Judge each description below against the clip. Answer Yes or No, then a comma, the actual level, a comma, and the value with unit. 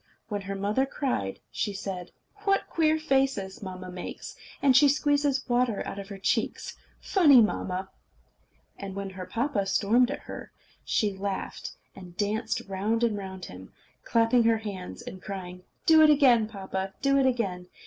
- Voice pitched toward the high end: Yes, high, 210 Hz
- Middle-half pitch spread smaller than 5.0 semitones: No, wide, 5.5 semitones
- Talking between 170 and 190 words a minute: No, average, 160 wpm